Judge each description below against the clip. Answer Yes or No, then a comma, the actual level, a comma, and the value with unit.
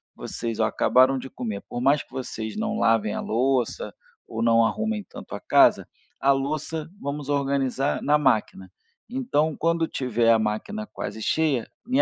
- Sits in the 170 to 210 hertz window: No, low, 135 Hz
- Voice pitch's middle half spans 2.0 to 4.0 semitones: No, average, 5.1 semitones